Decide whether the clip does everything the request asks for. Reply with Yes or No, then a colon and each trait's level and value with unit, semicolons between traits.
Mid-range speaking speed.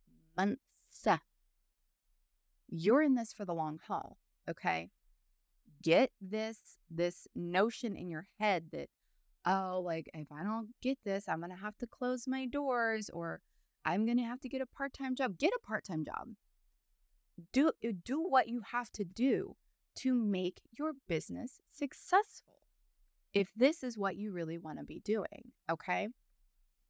Yes: average, 150 wpm